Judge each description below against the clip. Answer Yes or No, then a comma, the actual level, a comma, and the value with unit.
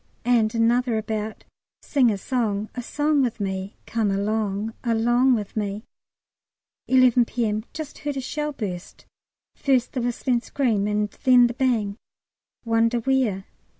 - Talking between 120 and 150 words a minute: Yes, average, 140 wpm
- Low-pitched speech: No, high, 230 Hz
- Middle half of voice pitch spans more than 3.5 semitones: No, average, 3.2 semitones